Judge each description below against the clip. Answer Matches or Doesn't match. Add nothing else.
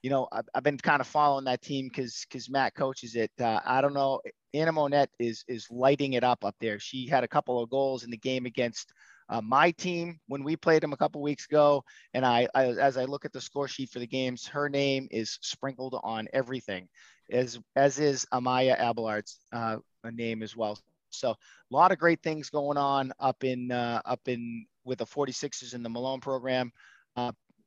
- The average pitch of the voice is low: Matches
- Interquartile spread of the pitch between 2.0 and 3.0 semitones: Matches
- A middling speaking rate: Doesn't match